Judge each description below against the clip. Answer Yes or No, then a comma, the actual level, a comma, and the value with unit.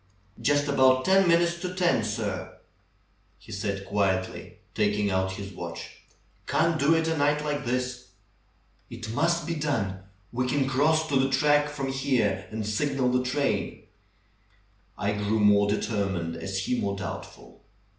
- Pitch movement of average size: No, wide, 6.3 semitones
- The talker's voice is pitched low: Yes, low, 125 Hz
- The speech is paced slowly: No, average, 150 wpm